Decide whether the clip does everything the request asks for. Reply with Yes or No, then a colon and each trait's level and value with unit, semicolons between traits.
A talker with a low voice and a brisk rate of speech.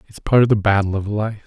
Yes: low, 105 Hz; fast, 285 wpm